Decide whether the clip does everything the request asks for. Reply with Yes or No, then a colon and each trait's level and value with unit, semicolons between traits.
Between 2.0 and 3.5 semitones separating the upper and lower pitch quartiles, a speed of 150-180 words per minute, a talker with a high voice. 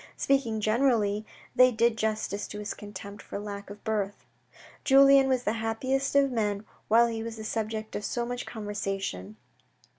Yes: average, 2.8 semitones; average, 160 wpm; high, 220 Hz